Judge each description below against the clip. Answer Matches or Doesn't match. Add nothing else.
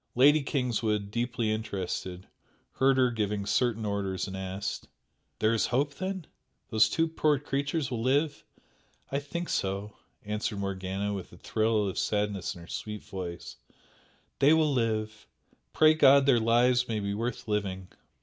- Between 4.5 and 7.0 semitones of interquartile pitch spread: Matches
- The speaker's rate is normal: Matches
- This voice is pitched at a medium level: Doesn't match